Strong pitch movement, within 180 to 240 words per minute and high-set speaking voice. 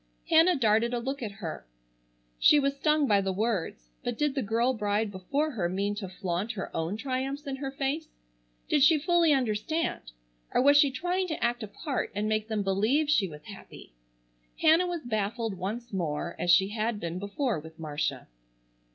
Yes: wide, 6.1 semitones; average, 185 wpm; high, 225 Hz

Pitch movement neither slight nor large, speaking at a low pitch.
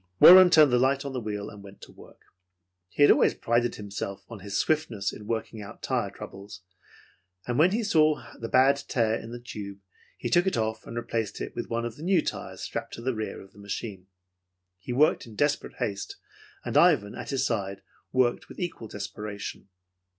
Yes: average, 4.8 semitones; low, 115 Hz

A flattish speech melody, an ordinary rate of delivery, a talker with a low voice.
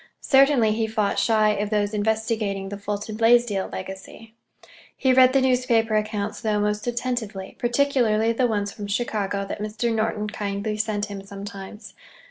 No: narrow, 2.1 semitones; average, 150 wpm; high, 215 Hz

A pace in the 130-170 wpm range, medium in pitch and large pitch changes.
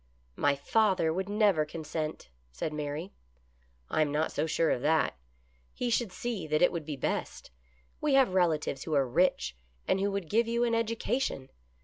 No: average, 190 wpm; medium, 165 Hz; wide, 5.8 semitones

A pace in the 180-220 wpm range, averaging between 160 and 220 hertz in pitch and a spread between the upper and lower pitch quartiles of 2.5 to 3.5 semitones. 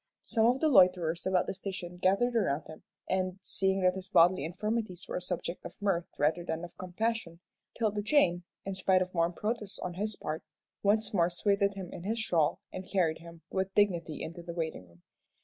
Yes: average, 200 wpm; medium, 185 Hz; average, 3.0 semitones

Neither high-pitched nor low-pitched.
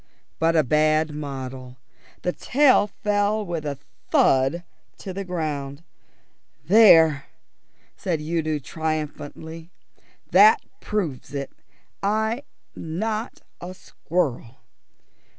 Yes: medium, 160 Hz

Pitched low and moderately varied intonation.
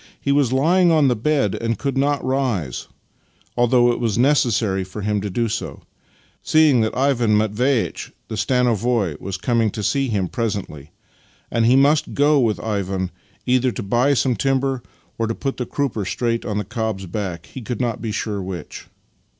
Yes: low, 115 Hz; average, 4.3 semitones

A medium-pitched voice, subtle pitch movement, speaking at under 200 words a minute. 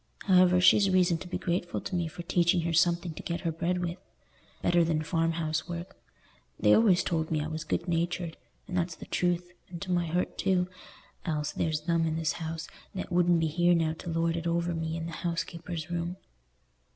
No: medium, 170 Hz; narrow, 1.4 semitones; fast, 205 wpm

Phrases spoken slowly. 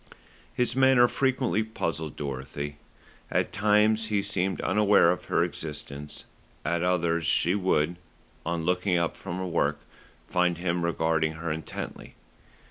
Yes: slow, 130 wpm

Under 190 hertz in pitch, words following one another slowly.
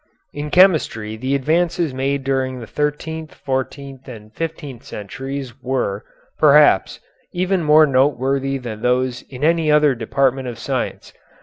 Yes: low, 135 Hz; slow, 130 wpm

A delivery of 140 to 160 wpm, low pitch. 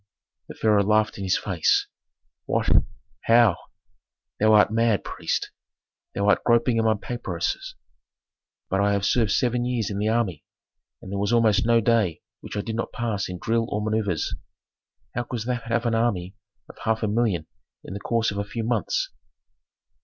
No: average, 175 wpm; low, 110 Hz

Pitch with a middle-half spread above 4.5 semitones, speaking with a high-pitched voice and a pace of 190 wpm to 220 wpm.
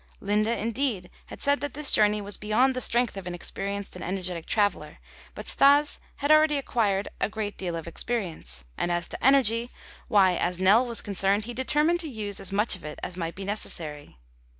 Yes: average, 5.0 semitones; high, 205 Hz; average, 195 wpm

